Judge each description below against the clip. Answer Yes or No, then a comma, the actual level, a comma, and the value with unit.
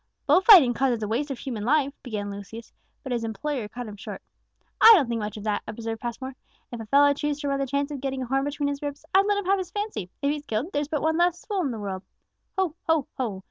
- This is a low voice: No, very high, 270 Hz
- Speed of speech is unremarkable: No, fast, 260 wpm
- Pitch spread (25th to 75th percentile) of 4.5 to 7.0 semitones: Yes, average, 4.8 semitones